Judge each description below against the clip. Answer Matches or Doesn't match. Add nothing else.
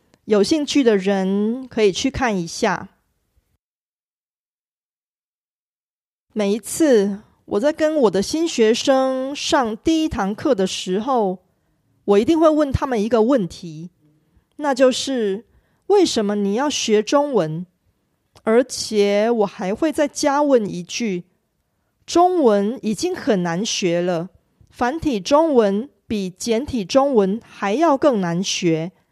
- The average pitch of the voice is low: Doesn't match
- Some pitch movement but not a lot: Doesn't match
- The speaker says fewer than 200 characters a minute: Matches